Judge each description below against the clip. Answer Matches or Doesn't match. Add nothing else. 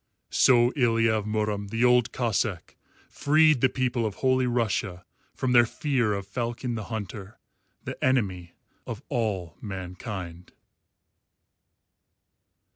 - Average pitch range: Matches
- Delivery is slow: Matches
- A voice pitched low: Matches